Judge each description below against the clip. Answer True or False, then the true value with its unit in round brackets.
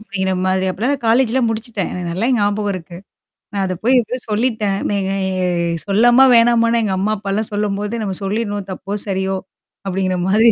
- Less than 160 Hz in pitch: False (205 Hz)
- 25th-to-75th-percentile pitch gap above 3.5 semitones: False (3.1 semitones)